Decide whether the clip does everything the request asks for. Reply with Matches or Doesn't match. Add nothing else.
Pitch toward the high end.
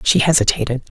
Doesn't match